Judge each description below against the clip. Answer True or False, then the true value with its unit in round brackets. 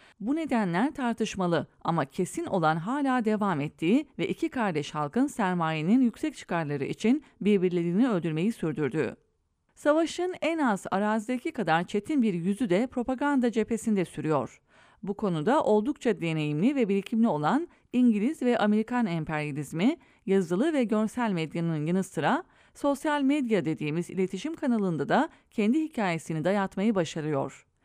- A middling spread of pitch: False (7.0 semitones)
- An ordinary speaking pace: False (125 wpm)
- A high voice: True (210 Hz)